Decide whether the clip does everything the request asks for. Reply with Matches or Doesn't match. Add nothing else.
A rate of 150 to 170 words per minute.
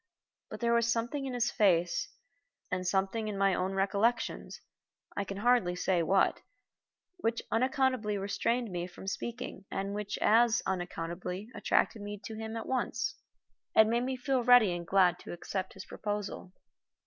Matches